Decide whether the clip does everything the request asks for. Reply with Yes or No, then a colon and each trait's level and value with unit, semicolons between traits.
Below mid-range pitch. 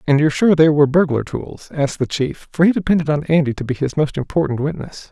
No: medium, 145 Hz